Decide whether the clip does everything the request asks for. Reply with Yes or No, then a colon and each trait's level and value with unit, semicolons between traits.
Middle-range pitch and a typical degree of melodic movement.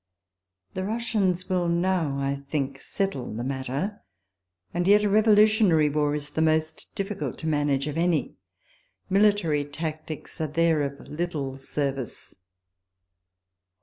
Yes: medium, 160 Hz; average, 4.6 semitones